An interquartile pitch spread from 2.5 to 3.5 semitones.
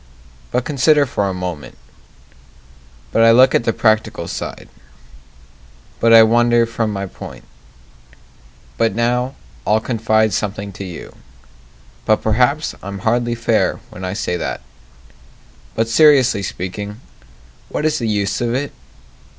Yes: average, 2.9 semitones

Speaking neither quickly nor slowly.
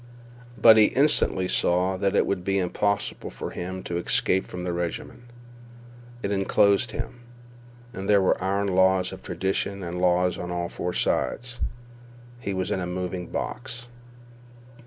Yes: average, 150 wpm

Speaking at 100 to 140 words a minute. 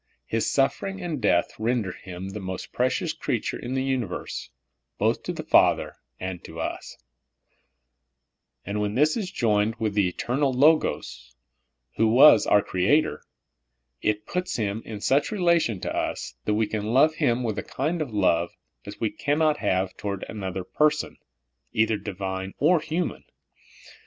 No: average, 150 wpm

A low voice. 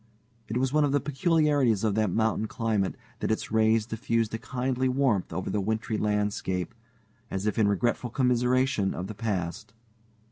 Yes: low, 110 Hz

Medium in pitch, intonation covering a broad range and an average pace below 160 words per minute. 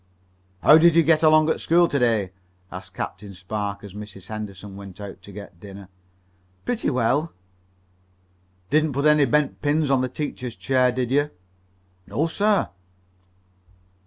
No: low, 125 Hz; wide, 7.2 semitones; average, 150 wpm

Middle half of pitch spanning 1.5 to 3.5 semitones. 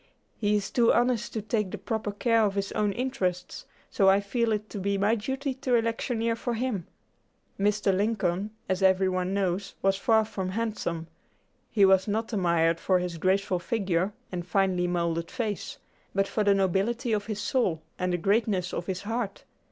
Yes: average, 3.2 semitones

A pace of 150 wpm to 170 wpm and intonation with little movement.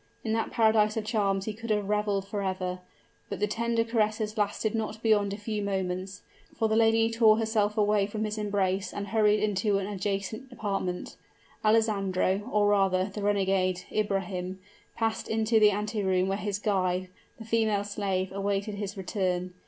Yes: average, 165 wpm; narrow, 2.0 semitones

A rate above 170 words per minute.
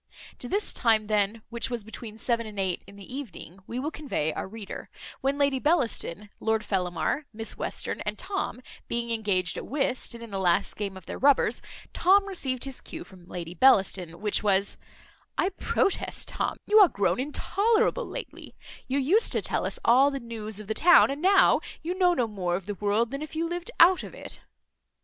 Yes: average, 200 wpm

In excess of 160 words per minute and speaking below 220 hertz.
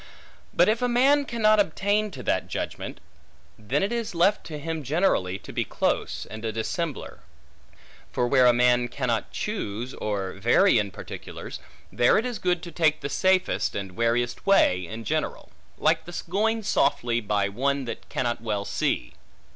Yes: average, 170 wpm; medium, 140 Hz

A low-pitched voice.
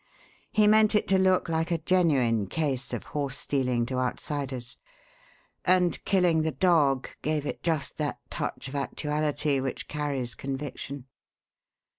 No: medium, 150 Hz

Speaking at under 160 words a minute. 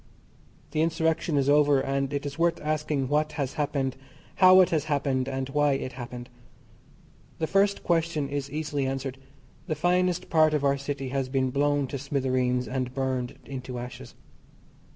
No: average, 165 wpm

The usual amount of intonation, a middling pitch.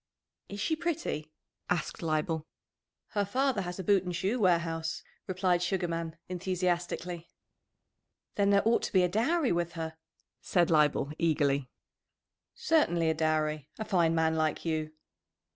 Yes: average, 3.4 semitones; medium, 175 Hz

